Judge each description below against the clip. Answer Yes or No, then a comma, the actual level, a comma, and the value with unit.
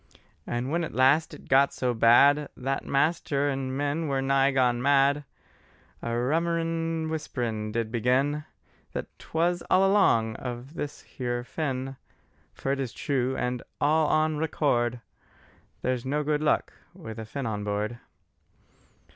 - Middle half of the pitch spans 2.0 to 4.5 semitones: Yes, average, 3.6 semitones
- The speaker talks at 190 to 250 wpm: No, average, 145 wpm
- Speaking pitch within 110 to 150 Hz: Yes, low, 135 Hz